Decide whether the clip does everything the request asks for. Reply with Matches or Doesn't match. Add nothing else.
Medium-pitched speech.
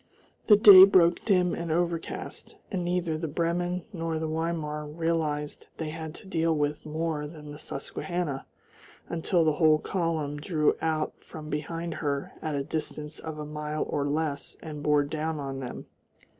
Matches